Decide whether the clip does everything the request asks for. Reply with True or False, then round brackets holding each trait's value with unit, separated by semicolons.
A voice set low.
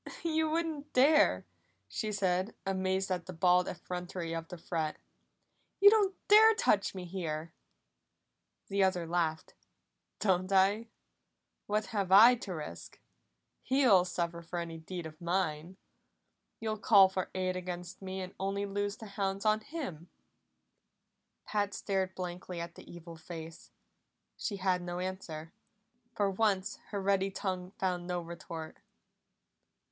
False (185 Hz)